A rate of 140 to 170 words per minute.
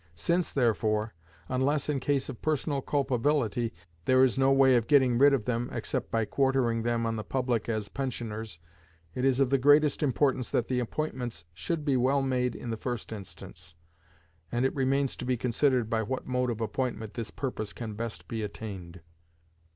No: average, 180 wpm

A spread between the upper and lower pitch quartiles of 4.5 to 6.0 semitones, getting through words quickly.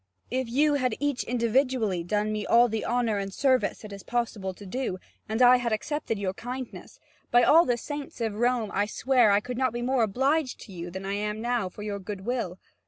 No: average, 3.6 semitones; fast, 225 wpm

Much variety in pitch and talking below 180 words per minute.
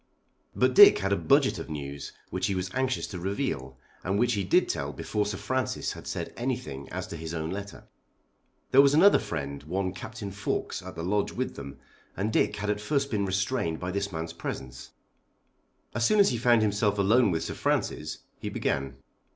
No: wide, 6.4 semitones; average, 200 wpm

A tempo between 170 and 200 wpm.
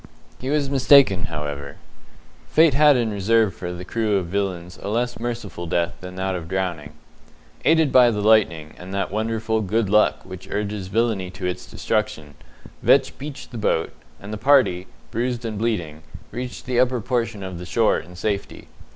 Yes: average, 175 wpm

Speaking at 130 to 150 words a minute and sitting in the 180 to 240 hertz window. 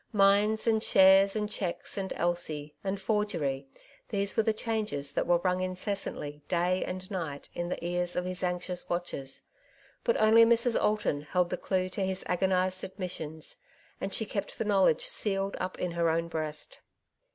No: average, 175 wpm; medium, 185 Hz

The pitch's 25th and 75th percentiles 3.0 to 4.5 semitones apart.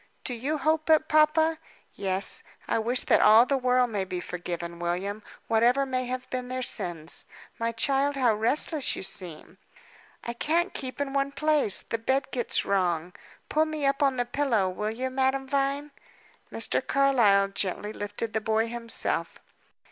No: average, 5.0 semitones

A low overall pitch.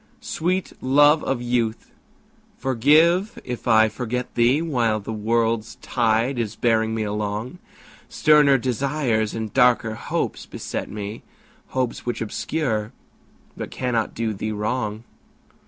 Yes: low, 120 Hz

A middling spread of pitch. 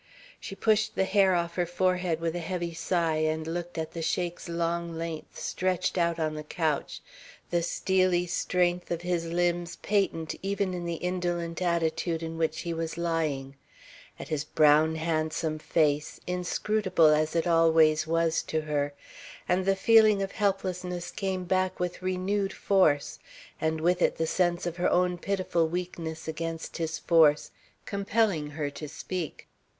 No: narrow, 2.2 semitones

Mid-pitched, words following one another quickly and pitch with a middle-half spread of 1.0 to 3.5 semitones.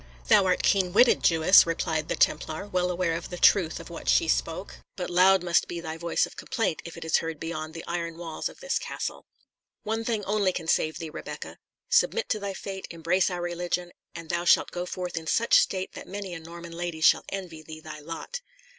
Yes: medium, 175 Hz; fast, 215 wpm; narrow, 2.5 semitones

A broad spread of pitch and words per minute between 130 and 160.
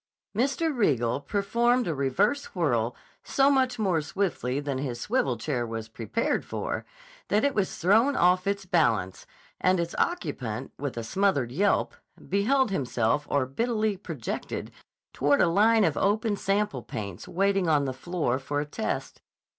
Yes: wide, 8.1 semitones; average, 150 wpm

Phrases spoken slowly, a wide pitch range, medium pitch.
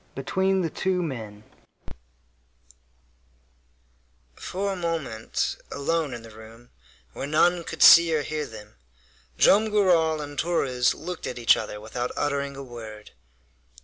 Yes: slow, 130 wpm; wide, 6.3 semitones; medium, 145 Hz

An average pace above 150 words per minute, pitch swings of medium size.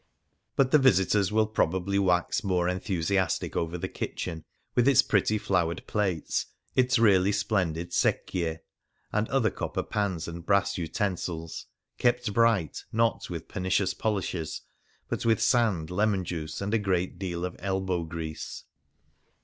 No: average, 140 wpm; average, 3.7 semitones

